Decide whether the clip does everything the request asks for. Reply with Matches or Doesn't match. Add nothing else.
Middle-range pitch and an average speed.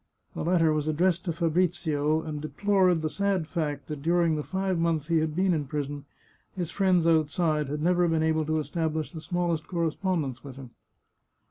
Matches